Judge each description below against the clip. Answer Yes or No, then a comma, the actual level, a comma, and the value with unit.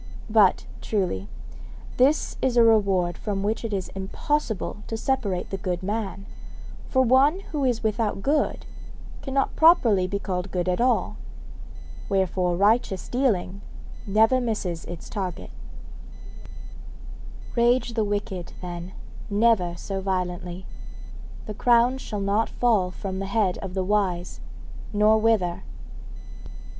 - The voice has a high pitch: Yes, high, 205 Hz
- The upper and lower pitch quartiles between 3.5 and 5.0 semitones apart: Yes, average, 4.0 semitones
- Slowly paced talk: Yes, slow, 125 wpm